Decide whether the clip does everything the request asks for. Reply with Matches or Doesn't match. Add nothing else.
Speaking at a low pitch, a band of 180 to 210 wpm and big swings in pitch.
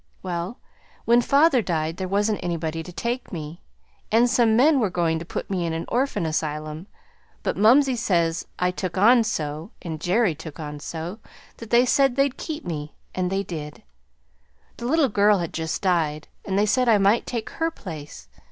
Doesn't match